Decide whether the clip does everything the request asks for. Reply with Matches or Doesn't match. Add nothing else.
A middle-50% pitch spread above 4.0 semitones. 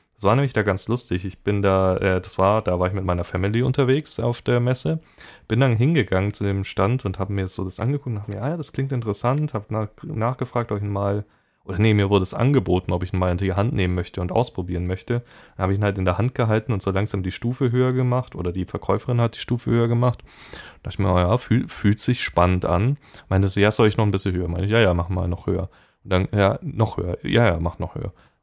Matches